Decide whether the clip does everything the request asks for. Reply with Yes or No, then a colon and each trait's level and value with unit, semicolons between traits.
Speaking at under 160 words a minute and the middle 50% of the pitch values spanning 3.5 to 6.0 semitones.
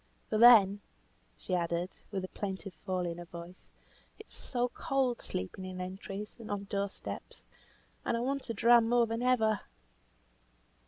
No: average, 165 wpm; average, 4.2 semitones